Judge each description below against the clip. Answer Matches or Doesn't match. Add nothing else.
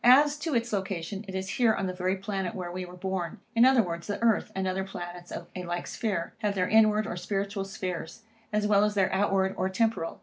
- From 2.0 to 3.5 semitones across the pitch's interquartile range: Matches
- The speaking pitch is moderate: Doesn't match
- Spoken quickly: Matches